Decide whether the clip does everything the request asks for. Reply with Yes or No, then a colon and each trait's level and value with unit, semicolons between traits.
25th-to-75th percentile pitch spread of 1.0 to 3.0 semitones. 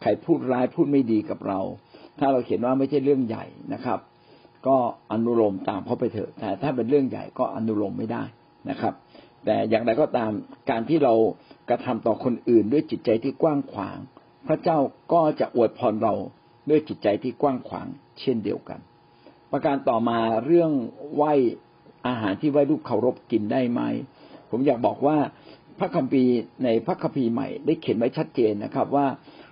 No: average, 3.9 semitones